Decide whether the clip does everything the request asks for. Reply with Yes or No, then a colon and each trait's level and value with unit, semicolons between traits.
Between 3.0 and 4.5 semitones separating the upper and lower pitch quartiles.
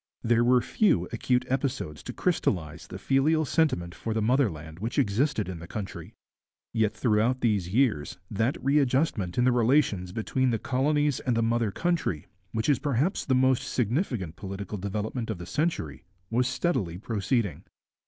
No: average, 5.1 semitones